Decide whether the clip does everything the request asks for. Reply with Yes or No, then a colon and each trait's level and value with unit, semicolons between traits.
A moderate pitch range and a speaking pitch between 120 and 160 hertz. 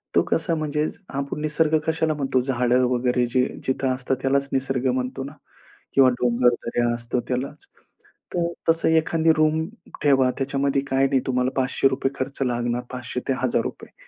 No: narrow, 2.3 semitones; low, 135 Hz